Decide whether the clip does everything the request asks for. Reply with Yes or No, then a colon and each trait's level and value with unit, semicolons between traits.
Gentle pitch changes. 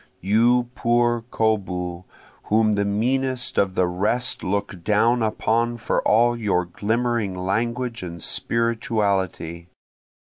No: average, 3.9 semitones